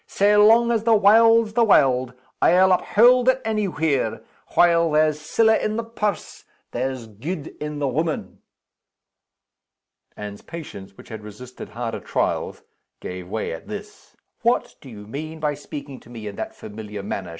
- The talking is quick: No, average, 160 wpm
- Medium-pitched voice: Yes, medium, 150 Hz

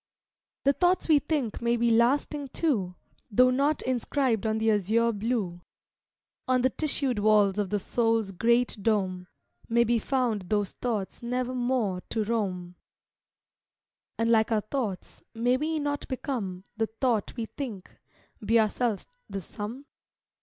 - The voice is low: No, high, 230 Hz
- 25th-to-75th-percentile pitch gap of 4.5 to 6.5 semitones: No, average, 3.5 semitones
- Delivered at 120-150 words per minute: Yes, average, 145 wpm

